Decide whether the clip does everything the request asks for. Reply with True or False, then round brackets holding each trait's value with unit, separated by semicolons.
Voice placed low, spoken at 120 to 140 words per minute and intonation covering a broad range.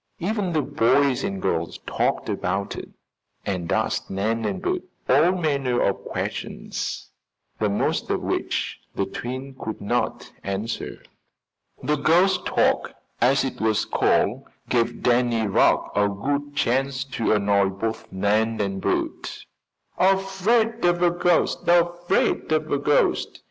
True (130 Hz; 135 wpm; 8.2 semitones)